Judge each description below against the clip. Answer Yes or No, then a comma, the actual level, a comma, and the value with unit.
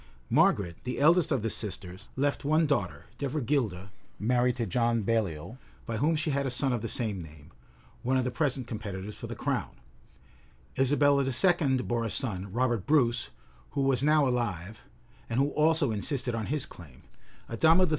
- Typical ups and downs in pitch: Yes, average, 4.7 semitones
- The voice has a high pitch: No, low, 125 Hz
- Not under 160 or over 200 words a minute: Yes, average, 175 wpm